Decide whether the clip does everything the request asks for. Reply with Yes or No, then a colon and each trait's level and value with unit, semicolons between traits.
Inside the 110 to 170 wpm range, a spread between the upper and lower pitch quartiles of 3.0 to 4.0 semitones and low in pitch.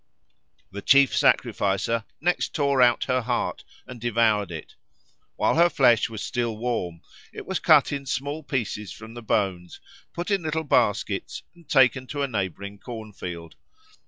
No: average, 160 wpm; average, 5.2 semitones; low, 120 Hz